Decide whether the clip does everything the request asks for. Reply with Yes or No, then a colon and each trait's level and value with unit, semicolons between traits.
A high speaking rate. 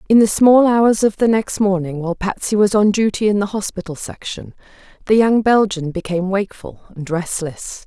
No: average, 185 wpm